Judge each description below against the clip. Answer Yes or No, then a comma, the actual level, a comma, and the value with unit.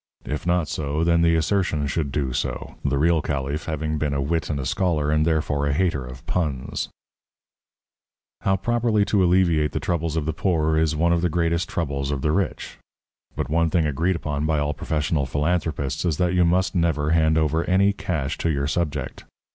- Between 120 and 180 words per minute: No, average, 195 wpm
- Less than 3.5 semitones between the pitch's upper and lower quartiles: Yes, average, 2.7 semitones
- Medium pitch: No, very low, 80 Hz